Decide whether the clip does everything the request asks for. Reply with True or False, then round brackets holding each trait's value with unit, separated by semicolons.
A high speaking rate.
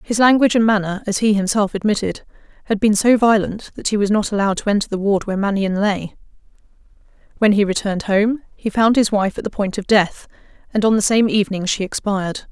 True (210 wpm)